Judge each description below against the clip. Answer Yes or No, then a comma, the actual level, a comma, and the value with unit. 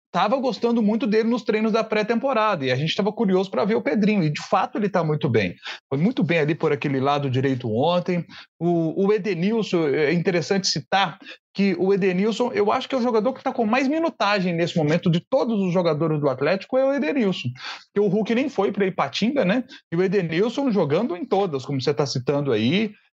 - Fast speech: Yes, fast, 215 wpm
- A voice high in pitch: Yes, high, 195 Hz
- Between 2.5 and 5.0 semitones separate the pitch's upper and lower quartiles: No, wide, 5.4 semitones